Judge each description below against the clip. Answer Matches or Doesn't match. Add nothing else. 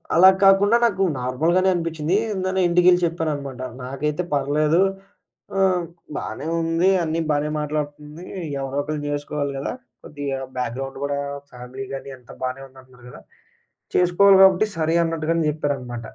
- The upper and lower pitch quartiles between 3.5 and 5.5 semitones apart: Matches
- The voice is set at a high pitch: Doesn't match